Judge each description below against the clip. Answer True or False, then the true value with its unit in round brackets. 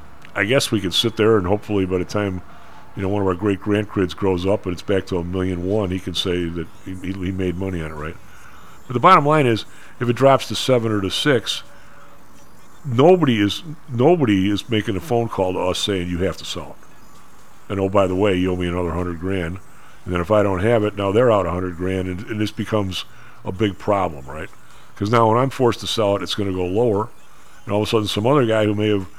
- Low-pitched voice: True (100 Hz)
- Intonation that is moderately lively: True (3.3 semitones)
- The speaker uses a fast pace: True (250 wpm)